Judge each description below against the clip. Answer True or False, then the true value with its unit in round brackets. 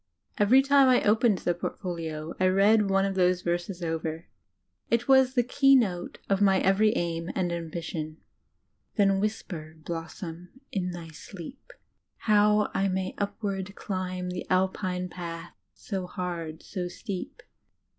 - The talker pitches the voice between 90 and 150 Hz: False (185 Hz)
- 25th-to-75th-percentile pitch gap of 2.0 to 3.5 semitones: True (3.1 semitones)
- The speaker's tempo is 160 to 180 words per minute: False (140 wpm)